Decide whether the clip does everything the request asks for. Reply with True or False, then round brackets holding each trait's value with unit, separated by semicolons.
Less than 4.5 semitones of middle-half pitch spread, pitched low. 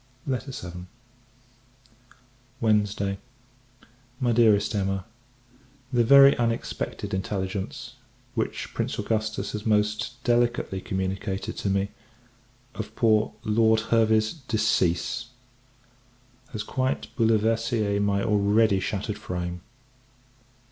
True (2.5 semitones; 110 Hz)